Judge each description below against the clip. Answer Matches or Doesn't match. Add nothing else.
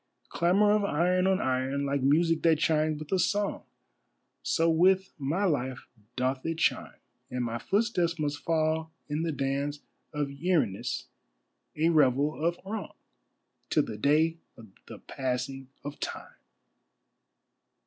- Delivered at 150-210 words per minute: Doesn't match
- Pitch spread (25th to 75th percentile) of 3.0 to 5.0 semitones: Matches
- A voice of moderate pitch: Matches